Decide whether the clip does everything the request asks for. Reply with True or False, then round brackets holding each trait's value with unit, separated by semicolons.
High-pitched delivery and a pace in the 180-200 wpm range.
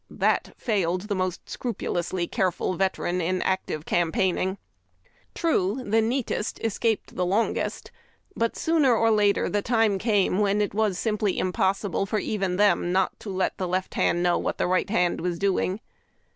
False (195 Hz; 170 wpm)